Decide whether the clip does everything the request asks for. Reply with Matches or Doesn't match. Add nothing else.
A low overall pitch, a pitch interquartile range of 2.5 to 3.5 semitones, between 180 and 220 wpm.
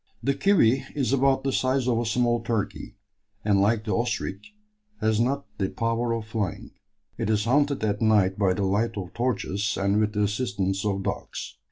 Matches